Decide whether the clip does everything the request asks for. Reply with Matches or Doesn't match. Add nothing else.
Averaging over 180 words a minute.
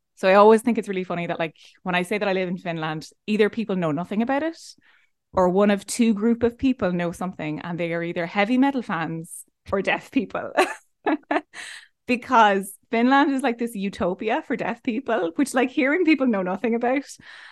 Matches